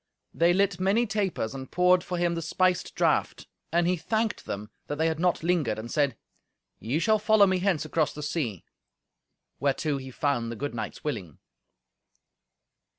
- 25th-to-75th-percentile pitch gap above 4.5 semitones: Yes, average, 4.9 semitones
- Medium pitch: Yes, medium, 165 Hz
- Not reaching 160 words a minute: No, average, 170 wpm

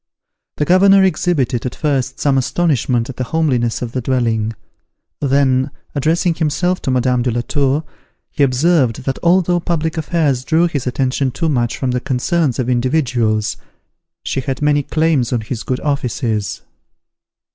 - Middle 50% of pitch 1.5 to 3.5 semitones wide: No, average, 4.3 semitones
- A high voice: No, low, 135 Hz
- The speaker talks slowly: No, average, 155 wpm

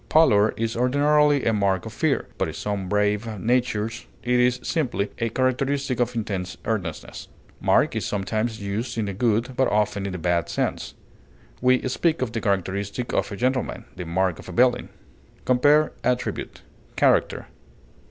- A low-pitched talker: Yes, low, 115 Hz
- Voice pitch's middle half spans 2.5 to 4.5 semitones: Yes, average, 4.0 semitones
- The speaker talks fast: No, average, 160 wpm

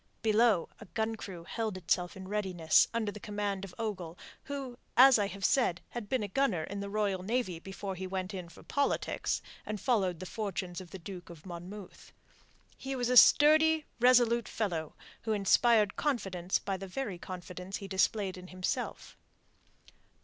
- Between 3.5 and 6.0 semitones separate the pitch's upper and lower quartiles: Yes, average, 3.9 semitones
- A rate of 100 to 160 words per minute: No, average, 170 wpm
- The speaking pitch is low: No, high, 200 Hz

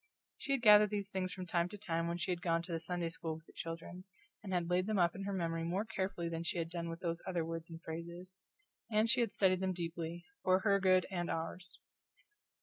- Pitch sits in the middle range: Yes, medium, 175 Hz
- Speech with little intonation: Yes, narrow, 2.3 semitones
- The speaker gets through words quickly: Yes, fast, 240 wpm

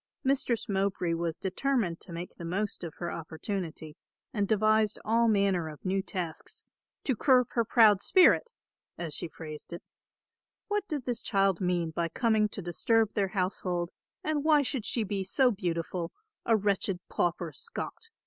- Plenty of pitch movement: No, average, 4.7 semitones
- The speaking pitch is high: Yes, high, 195 Hz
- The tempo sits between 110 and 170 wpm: Yes, average, 160 wpm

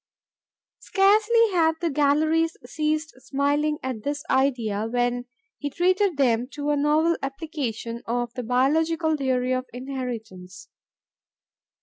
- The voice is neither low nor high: No, very high, 280 Hz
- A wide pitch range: No, average, 4.3 semitones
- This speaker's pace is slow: Yes, slow, 115 wpm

